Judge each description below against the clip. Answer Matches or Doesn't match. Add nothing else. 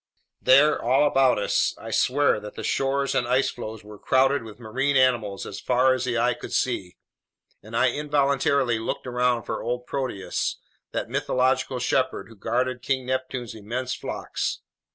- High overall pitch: Doesn't match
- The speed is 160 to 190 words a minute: Matches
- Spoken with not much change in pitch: Matches